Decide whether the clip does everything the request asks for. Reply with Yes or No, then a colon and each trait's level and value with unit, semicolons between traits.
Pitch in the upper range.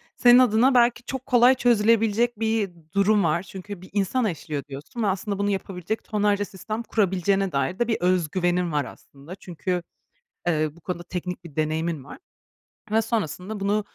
Yes: high, 195 Hz